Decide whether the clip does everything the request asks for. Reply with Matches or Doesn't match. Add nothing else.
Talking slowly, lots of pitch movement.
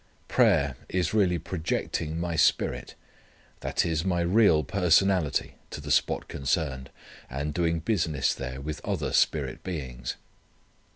Doesn't match